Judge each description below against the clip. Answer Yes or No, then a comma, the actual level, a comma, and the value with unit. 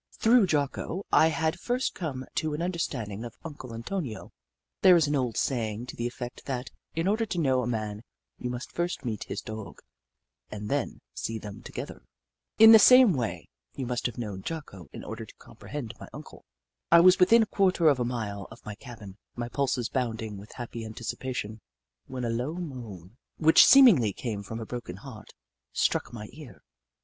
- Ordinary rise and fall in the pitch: No, wide, 6.5 semitones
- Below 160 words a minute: No, average, 190 wpm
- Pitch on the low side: Yes, low, 125 Hz